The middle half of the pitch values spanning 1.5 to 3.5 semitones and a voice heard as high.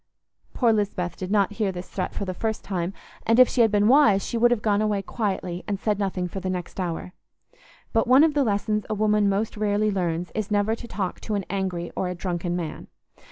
Yes: average, 2.9 semitones; high, 205 Hz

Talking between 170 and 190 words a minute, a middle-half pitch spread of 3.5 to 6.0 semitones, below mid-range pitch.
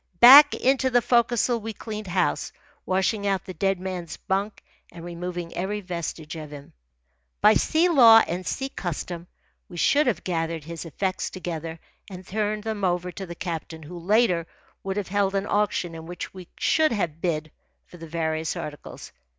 No: average, 175 wpm; average, 4.0 semitones; medium, 185 Hz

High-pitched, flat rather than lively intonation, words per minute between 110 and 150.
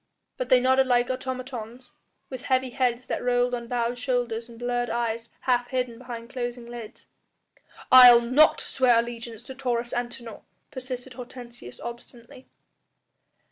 Yes: high, 245 Hz; narrow, 1.4 semitones; average, 140 wpm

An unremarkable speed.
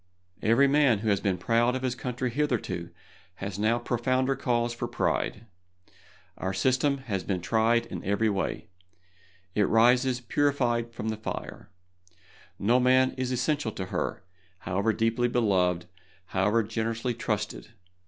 Yes: average, 145 wpm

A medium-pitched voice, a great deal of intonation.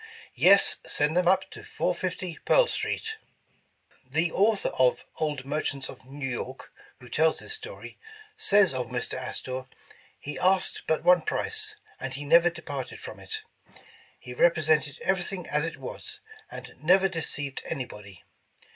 Yes: medium, 160 Hz; wide, 5.7 semitones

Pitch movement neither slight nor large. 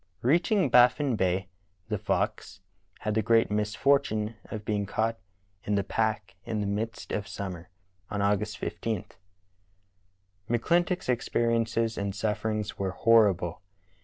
No: narrow, 2.3 semitones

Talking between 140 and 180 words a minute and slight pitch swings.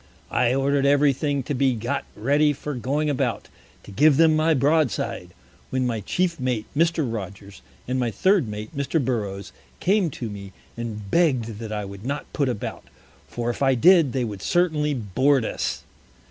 No: average, 175 wpm; average, 4.9 semitones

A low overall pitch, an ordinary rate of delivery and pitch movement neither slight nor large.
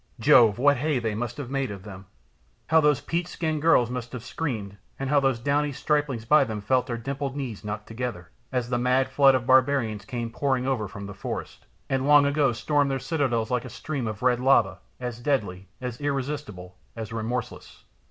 Yes: low, 125 Hz; average, 195 wpm; average, 3.8 semitones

